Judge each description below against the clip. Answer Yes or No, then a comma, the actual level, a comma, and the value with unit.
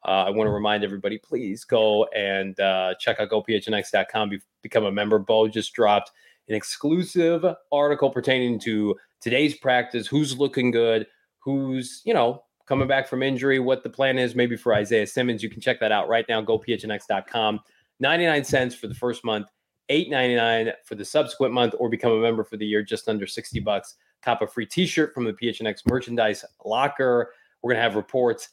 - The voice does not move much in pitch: No, average, 3.6 semitones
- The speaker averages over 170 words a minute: Yes, average, 190 wpm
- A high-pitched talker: No, low, 120 Hz